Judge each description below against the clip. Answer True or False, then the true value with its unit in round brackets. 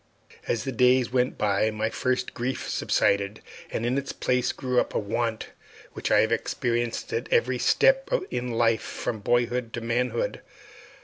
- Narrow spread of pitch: True (1.9 semitones)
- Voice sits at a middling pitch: False (120 Hz)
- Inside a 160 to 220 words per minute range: True (165 wpm)